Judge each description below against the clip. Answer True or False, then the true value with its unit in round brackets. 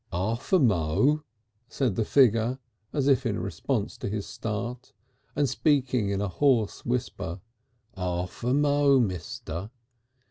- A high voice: False (115 Hz)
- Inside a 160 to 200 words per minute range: False (135 wpm)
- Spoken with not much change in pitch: False (5.5 semitones)